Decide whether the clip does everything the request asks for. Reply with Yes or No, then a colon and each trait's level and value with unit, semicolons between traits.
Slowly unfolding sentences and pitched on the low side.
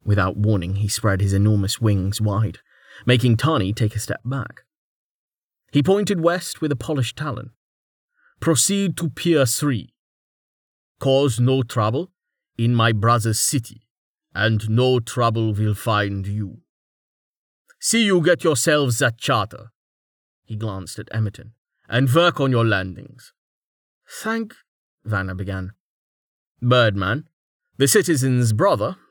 Yes: slow, 125 wpm; low, 115 Hz